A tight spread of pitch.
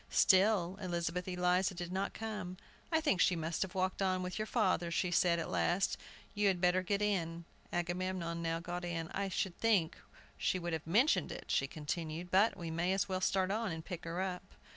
Yes: narrow, 2.2 semitones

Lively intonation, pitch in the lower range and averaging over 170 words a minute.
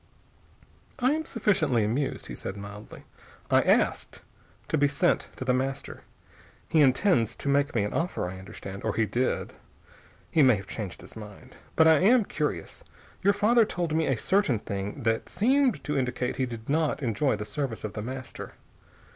Yes: wide, 6.7 semitones; low, 130 Hz; average, 180 wpm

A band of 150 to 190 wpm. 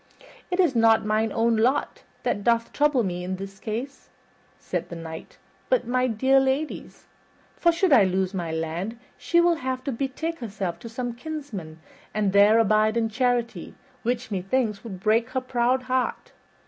Yes: average, 170 wpm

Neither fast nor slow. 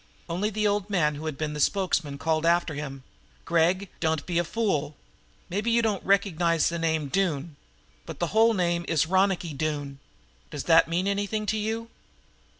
Yes: average, 180 wpm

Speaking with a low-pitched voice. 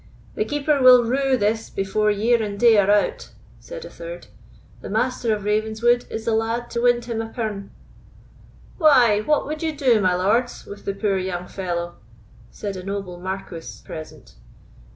No: high, 220 Hz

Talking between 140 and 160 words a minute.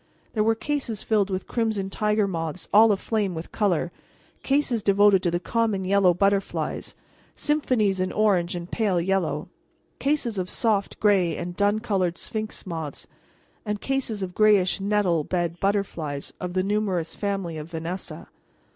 Yes: average, 150 wpm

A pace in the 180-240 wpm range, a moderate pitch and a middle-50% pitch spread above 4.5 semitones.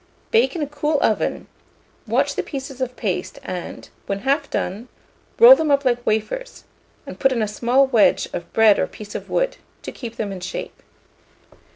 No: average, 185 wpm; high, 245 Hz; average, 5.1 semitones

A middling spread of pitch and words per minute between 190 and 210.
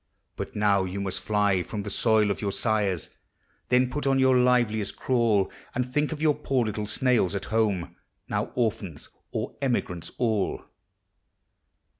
No: average, 4.0 semitones; average, 155 wpm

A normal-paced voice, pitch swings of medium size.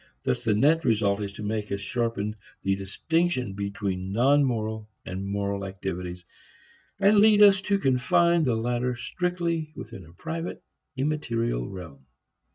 No: average, 150 wpm; wide, 7.5 semitones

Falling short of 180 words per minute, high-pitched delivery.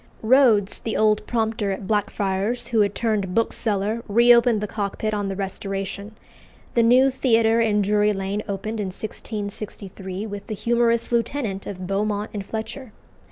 Yes: average, 150 wpm; high, 210 Hz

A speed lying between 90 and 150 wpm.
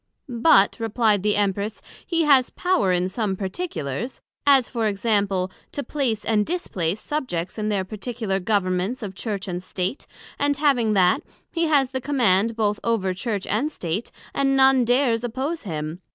No: average, 160 wpm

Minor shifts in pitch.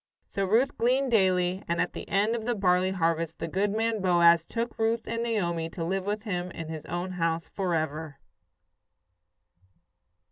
No: average, 4.6 semitones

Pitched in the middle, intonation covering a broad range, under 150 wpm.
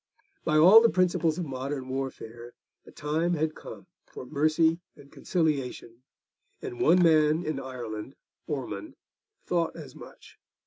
No: medium, 155 Hz; average, 4.3 semitones; slow, 135 wpm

